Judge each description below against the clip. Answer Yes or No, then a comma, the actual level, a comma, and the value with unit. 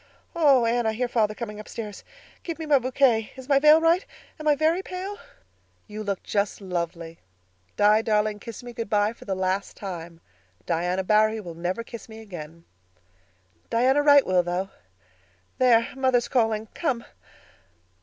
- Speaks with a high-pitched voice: Yes, high, 220 Hz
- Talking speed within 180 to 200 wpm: No, average, 160 wpm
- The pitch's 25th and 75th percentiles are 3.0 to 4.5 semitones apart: No, average, 4.9 semitones